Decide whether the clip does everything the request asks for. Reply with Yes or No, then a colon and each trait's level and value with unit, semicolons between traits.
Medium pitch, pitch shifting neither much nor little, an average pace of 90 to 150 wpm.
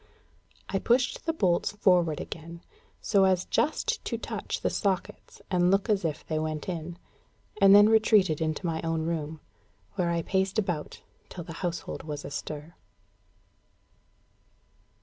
Yes: medium, 175 Hz; average, 3.4 semitones; average, 145 wpm